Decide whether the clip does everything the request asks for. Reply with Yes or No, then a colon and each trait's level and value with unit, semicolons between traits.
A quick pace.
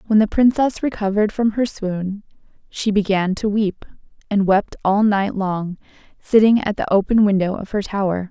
No: average, 175 wpm